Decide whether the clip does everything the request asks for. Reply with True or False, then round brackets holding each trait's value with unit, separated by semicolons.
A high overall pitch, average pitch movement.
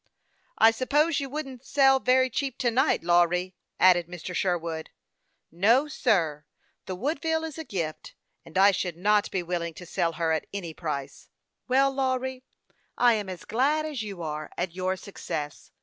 False (200 Hz; 7.4 semitones)